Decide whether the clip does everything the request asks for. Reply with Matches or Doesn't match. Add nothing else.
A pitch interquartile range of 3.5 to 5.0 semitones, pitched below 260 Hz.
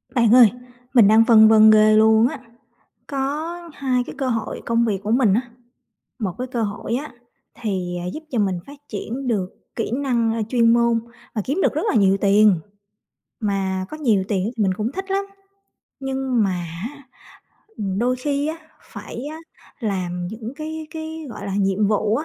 Matches